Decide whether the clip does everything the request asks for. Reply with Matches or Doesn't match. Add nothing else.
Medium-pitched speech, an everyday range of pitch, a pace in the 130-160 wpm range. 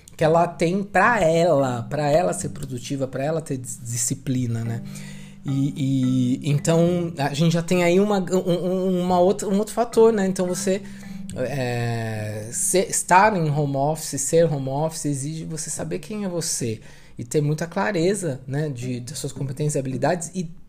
Doesn't match